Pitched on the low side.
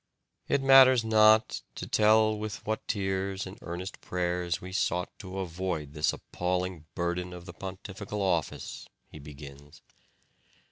Yes: very low, 95 Hz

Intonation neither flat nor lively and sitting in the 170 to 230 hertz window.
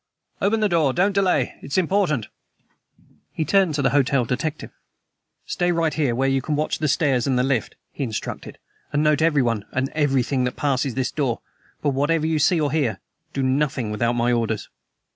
No: average, 3.7 semitones; medium, 140 Hz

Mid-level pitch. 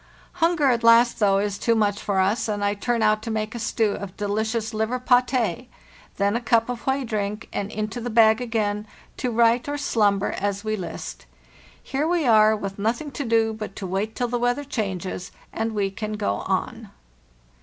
No: high, 220 Hz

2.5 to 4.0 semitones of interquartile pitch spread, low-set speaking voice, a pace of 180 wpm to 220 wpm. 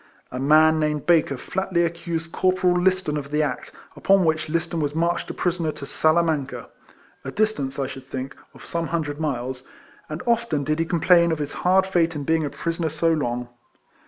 No: average, 2.8 semitones; medium, 160 Hz; average, 190 wpm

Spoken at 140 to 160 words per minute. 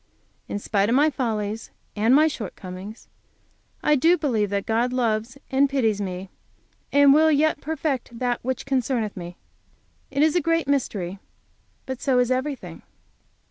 Yes: average, 150 wpm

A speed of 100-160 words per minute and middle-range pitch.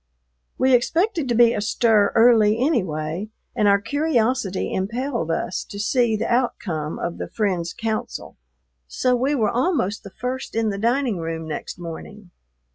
No: average, 150 wpm; high, 220 Hz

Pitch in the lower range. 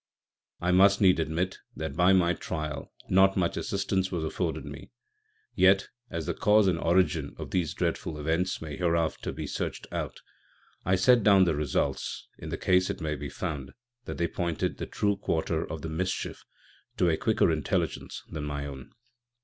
Yes: very low, 85 Hz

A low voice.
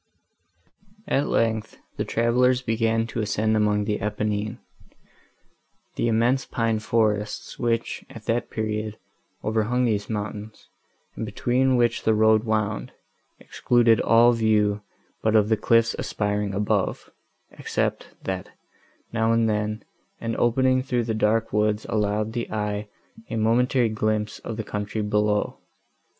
Yes: low, 110 Hz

